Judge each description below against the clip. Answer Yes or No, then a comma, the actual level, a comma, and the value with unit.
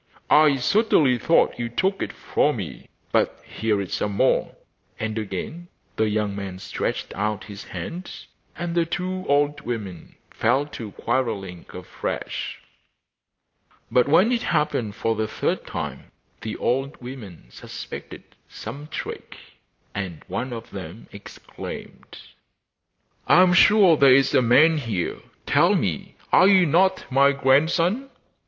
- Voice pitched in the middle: No, low, 130 Hz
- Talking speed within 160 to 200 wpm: No, slow, 135 wpm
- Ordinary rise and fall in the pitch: No, wide, 7.5 semitones